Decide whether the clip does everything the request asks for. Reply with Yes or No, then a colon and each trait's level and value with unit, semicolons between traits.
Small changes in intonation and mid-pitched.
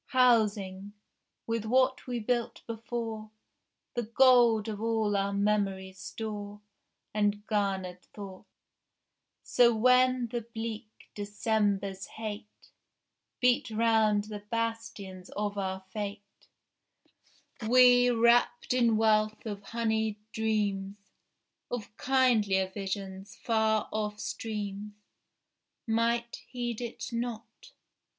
No: narrow, 2.3 semitones; high, 220 Hz